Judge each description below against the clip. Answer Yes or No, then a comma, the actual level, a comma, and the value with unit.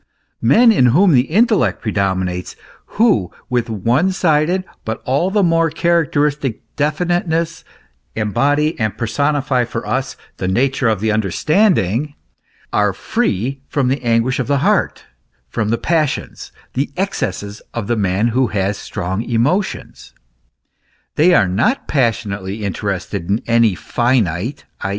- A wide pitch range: Yes, wide, 6.4 semitones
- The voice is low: Yes, low, 125 Hz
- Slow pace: Yes, slow, 130 wpm